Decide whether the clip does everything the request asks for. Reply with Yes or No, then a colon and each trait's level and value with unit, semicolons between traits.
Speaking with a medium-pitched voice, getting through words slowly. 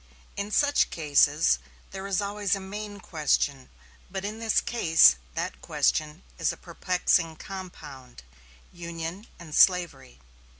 Yes: medium, 175 Hz; slow, 125 wpm